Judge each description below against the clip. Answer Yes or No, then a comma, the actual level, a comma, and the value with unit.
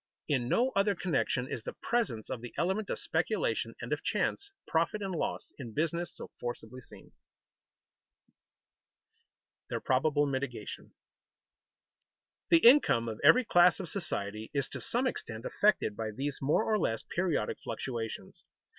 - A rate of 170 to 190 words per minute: No, average, 145 wpm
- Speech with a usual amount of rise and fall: No, wide, 8.7 semitones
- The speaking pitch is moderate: Yes, medium, 145 Hz